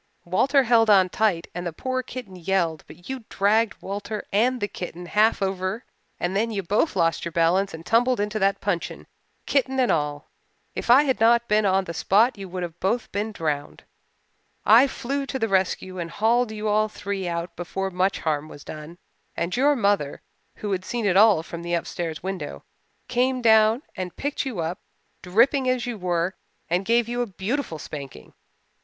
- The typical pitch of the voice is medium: No, high, 200 Hz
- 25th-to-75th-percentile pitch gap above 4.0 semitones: Yes, average, 5.0 semitones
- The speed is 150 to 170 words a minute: No, average, 190 wpm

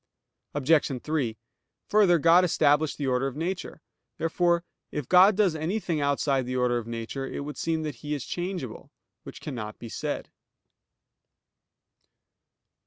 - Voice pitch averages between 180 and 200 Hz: No, medium, 150 Hz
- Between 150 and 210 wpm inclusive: No, average, 140 wpm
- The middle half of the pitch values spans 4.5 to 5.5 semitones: Yes, average, 4.9 semitones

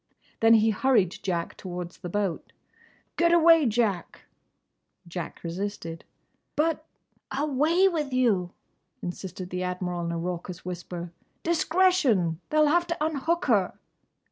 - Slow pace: Yes, slow, 115 wpm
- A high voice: Yes, high, 205 Hz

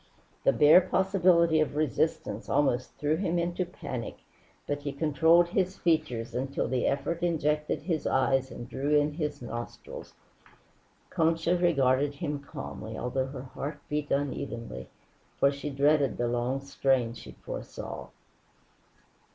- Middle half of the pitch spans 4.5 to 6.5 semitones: No, average, 3.7 semitones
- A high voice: No, medium, 145 Hz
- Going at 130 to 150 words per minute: Yes, slow, 135 wpm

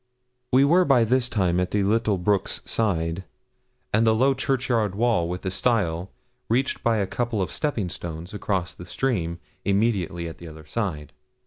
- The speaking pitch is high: No, low, 100 Hz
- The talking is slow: No, average, 175 wpm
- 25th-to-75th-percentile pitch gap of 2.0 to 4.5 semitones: No, average, 5.2 semitones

